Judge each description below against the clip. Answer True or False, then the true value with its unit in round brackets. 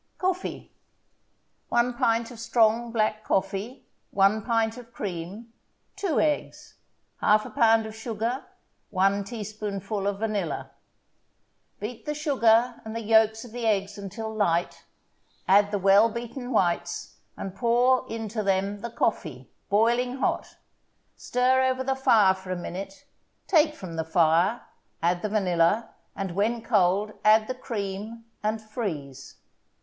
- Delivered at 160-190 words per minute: False (135 wpm)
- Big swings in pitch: False (3.2 semitones)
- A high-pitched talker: True (220 Hz)